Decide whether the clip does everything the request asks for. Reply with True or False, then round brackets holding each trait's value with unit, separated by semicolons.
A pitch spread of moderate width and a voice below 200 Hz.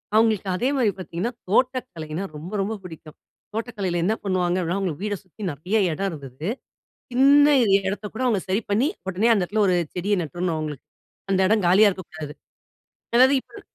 True (4.2 semitones; 190 Hz)